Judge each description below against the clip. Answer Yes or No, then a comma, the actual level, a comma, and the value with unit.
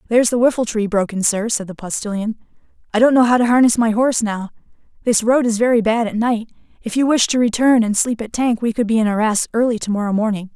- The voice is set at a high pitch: Yes, high, 225 Hz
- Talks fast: Yes, fast, 245 wpm